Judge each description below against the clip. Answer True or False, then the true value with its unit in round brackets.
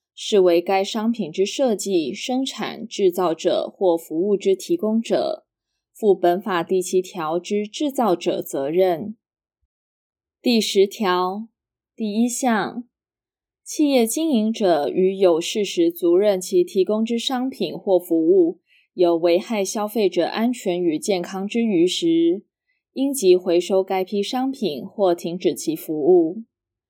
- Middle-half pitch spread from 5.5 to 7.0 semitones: False (5.1 semitones)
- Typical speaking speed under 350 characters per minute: True (190 characters per minute)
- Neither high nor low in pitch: False (200 Hz)